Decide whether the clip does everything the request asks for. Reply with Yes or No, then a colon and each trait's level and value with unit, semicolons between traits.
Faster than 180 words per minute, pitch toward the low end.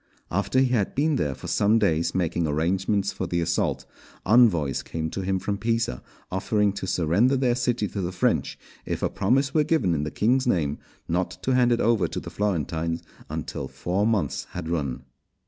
Yes: average, 190 wpm; very low, 95 Hz